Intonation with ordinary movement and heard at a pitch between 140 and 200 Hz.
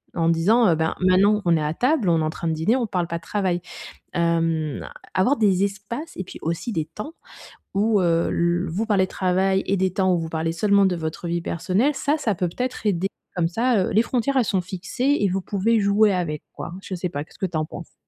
Yes: average, 3.9 semitones; medium, 185 Hz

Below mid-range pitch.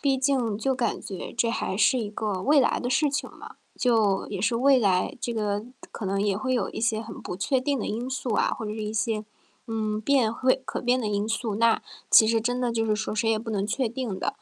No: high, 225 Hz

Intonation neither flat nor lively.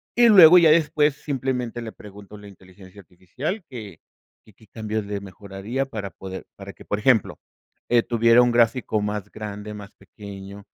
Yes: average, 3.8 semitones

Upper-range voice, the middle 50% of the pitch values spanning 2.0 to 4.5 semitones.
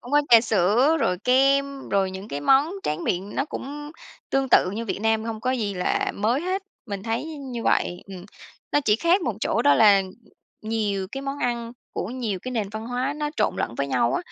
No: high, 230 Hz; wide, 5.4 semitones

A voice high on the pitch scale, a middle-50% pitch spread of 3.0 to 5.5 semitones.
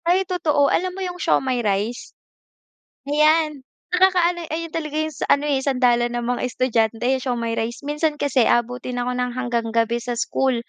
Yes: very high, 255 Hz; average, 4.6 semitones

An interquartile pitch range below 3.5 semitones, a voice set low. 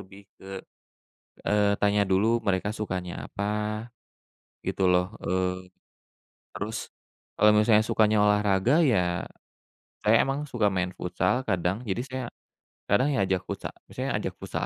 Yes: narrow, 2.6 semitones; low, 105 Hz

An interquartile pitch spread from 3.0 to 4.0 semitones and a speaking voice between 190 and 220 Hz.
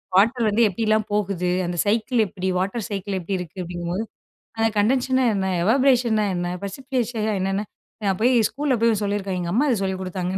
Yes: average, 3.7 semitones; high, 205 Hz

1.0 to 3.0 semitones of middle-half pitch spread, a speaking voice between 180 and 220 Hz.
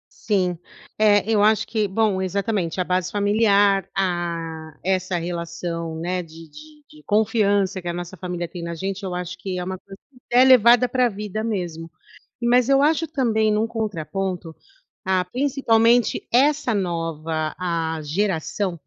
No: average, 4.2 semitones; high, 190 Hz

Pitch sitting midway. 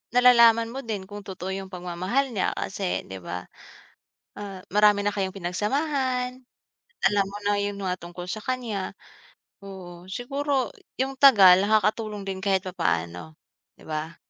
No: high, 200 Hz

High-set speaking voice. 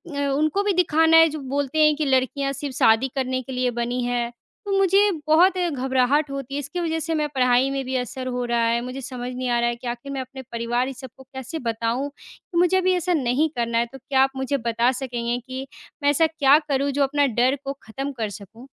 Yes: very high, 265 Hz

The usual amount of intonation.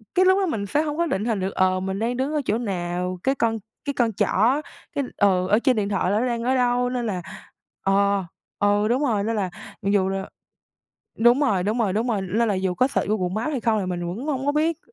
Yes: average, 4.6 semitones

